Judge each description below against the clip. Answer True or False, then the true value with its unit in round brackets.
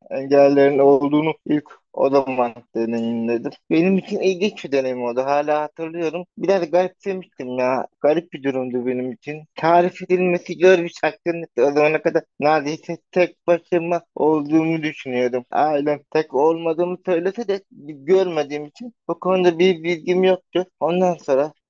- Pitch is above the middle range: False (160 Hz)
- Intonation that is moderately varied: True (4.0 semitones)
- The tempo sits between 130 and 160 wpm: True (135 wpm)